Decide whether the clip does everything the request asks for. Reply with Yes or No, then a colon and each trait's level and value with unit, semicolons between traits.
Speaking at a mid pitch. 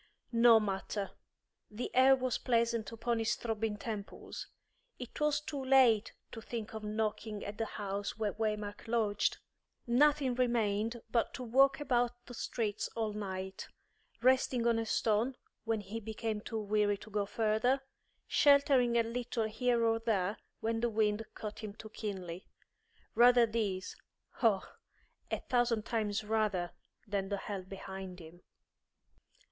No: high, 225 Hz